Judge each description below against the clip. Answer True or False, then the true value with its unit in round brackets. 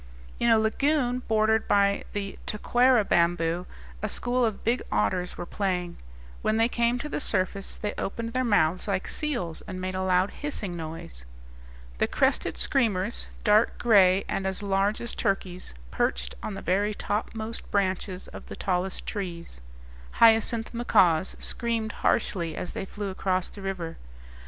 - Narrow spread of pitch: False (3.6 semitones)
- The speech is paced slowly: False (155 wpm)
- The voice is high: True (200 Hz)